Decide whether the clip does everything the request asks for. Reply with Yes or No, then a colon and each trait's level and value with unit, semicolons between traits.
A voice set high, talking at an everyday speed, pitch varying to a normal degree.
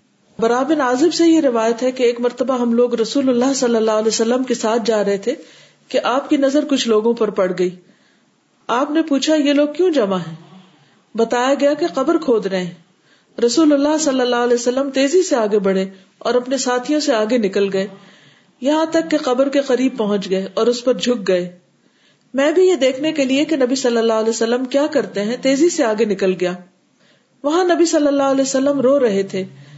No: high, 245 Hz; fast, 210 wpm; average, 4.6 semitones